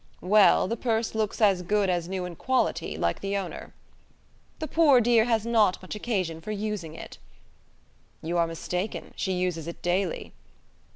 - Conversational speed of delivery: Yes, average, 165 wpm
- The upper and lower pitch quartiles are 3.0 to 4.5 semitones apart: Yes, average, 3.8 semitones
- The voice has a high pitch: Yes, high, 195 Hz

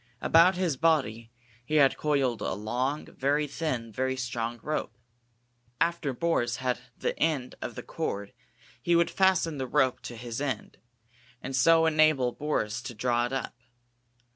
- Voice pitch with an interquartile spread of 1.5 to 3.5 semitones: No, average, 4.4 semitones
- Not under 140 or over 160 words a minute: Yes, average, 155 wpm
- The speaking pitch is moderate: No, low, 130 Hz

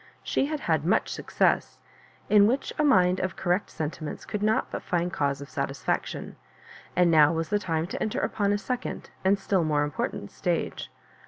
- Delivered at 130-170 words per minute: No, average, 185 wpm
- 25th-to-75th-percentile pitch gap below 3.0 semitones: No, average, 4.7 semitones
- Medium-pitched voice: Yes, medium, 180 Hz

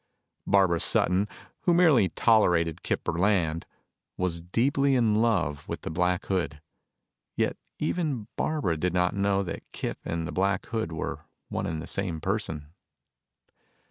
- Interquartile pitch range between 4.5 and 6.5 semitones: Yes, average, 4.8 semitones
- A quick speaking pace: No, average, 140 wpm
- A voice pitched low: Yes, very low, 95 Hz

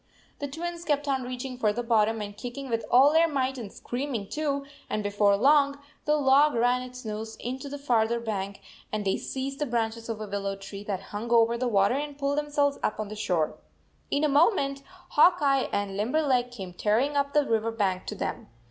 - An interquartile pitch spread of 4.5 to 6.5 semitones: Yes, average, 4.8 semitones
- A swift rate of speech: Yes, fast, 210 wpm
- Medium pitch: No, high, 245 Hz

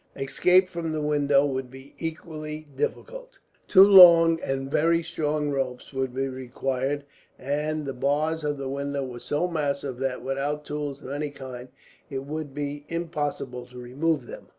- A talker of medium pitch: Yes, medium, 145 Hz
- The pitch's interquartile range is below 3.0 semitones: Yes, narrow, 2.6 semitones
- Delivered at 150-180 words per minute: Yes, average, 160 wpm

